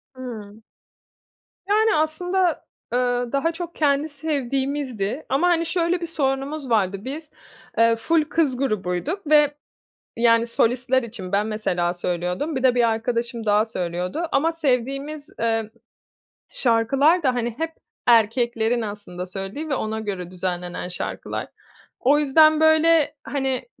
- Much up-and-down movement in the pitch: Yes, wide, 5.9 semitones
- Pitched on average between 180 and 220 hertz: No, very high, 255 Hz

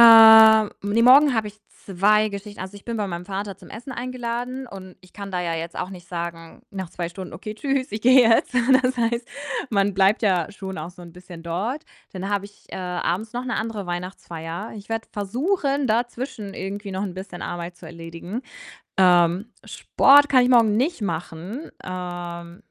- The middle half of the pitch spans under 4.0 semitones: No, average, 4.5 semitones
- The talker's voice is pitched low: No, high, 200 Hz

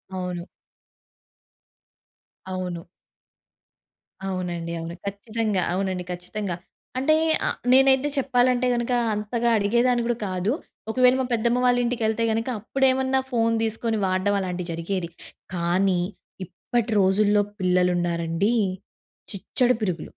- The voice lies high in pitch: Yes, high, 205 Hz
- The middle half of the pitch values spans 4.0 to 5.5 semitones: Yes, average, 4.9 semitones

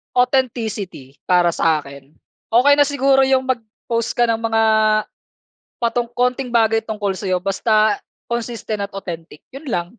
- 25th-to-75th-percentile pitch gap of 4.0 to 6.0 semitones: Yes, average, 4.4 semitones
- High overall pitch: Yes, high, 225 Hz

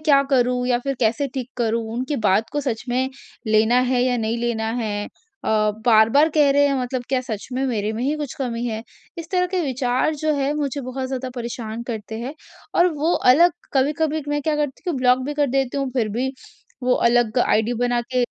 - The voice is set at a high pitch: Yes, very high, 255 Hz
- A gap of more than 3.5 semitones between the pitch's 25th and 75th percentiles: No, average, 3.2 semitones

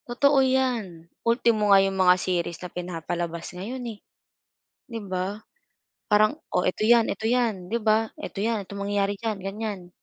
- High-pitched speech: Yes, high, 205 Hz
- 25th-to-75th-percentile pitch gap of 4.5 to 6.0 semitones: No, average, 3.8 semitones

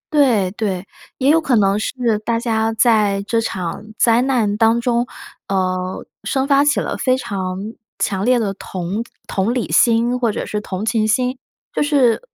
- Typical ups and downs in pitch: Yes, average, 3.9 semitones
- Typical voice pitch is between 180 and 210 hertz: No, high, 225 Hz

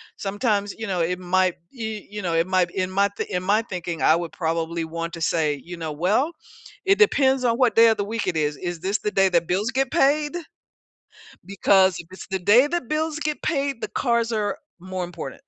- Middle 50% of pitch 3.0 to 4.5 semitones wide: No, average, 5.1 semitones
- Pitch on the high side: Yes, high, 195 Hz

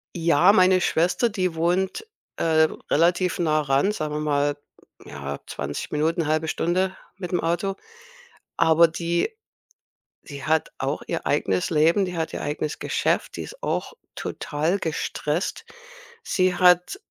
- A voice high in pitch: No, medium, 165 Hz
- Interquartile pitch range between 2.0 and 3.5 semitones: Yes, average, 3.1 semitones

